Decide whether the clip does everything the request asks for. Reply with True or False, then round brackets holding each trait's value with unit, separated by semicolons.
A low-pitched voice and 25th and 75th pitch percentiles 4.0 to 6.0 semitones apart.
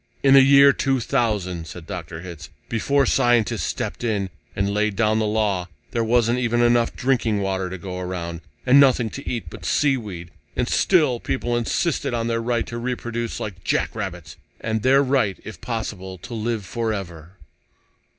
True (110 Hz; 4.3 semitones)